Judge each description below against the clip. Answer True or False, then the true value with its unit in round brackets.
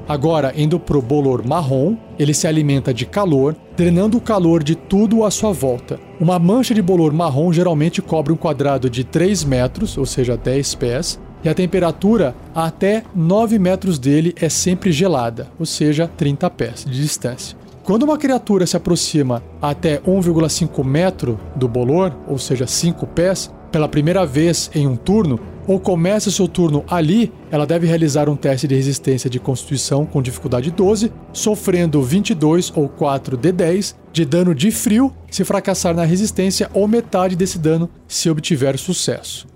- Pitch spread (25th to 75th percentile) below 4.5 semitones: False (4.8 semitones)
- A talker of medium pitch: True (165 Hz)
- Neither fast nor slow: True (165 wpm)